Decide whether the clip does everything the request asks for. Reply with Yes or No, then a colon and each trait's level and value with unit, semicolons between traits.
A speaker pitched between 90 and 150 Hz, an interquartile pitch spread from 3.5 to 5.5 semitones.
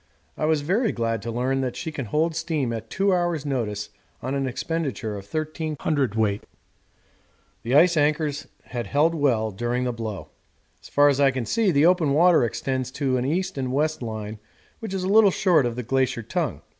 Yes: medium, 140 Hz; average, 5.1 semitones